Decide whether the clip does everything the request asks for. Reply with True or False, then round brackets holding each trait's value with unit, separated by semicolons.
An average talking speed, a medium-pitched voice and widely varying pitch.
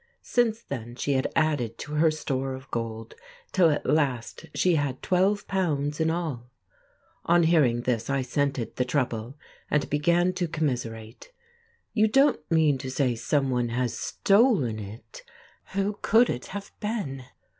True (145 wpm; 145 Hz; 5.8 semitones)